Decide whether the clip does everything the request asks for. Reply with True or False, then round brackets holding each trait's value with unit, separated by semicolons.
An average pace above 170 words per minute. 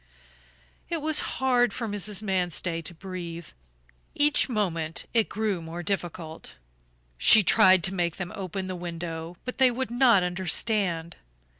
False (140 wpm)